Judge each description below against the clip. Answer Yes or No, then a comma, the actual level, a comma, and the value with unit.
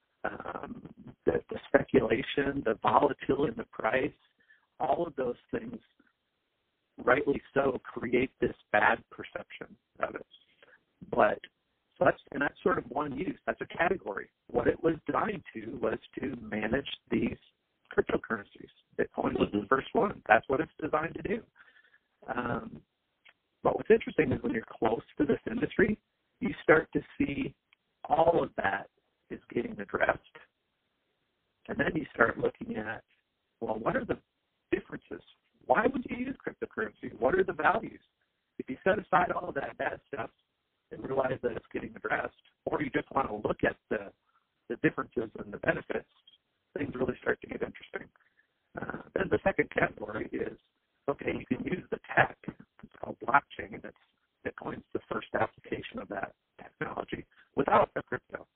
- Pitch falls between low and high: Yes, medium, 160 Hz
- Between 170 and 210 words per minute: No, average, 160 wpm